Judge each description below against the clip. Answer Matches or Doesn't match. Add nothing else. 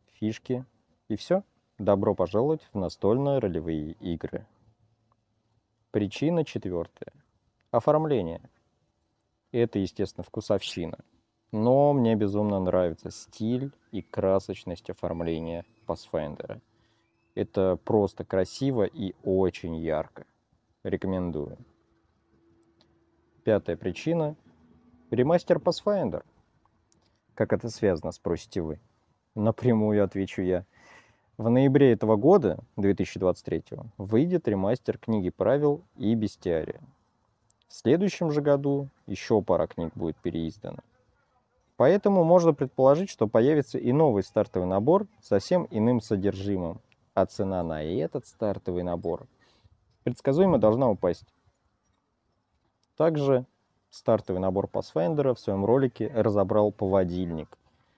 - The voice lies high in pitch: Doesn't match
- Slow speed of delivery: Matches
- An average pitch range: Matches